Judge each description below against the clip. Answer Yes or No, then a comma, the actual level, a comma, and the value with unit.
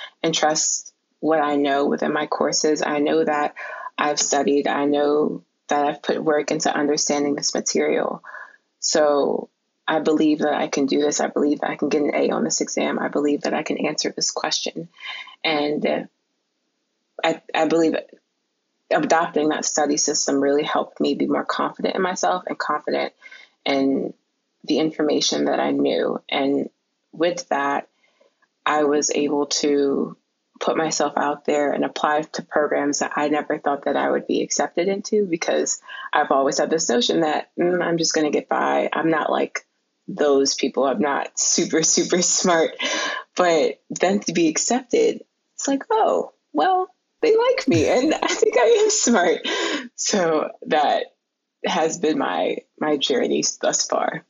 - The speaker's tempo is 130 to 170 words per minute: Yes, average, 165 wpm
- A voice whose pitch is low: No, medium, 150 Hz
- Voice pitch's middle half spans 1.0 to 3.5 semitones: Yes, average, 3.1 semitones